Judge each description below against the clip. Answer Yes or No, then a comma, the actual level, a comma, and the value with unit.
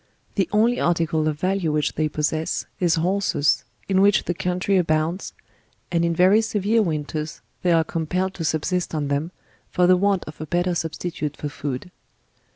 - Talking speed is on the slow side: No, average, 190 wpm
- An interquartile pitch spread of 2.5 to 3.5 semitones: Yes, average, 3.1 semitones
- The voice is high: No, medium, 170 Hz